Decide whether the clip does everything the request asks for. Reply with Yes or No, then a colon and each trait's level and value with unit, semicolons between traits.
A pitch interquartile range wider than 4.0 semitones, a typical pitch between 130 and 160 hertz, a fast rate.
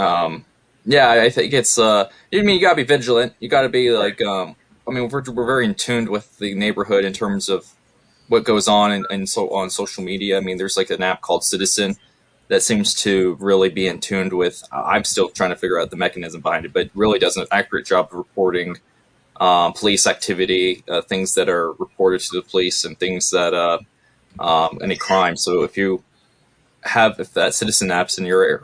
No: average, 4.8 semitones; low, 100 Hz; fast, 215 wpm